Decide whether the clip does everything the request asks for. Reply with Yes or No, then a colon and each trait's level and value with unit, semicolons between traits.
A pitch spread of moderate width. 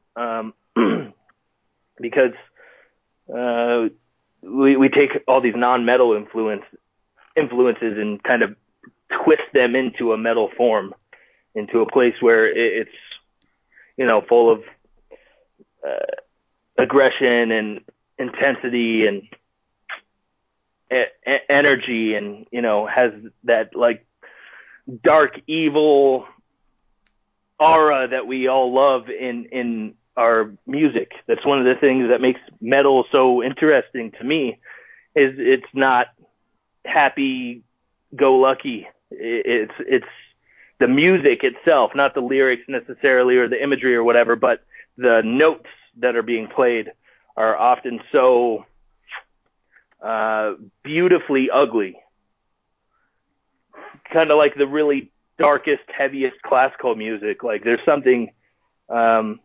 Yes: average, 4.9 semitones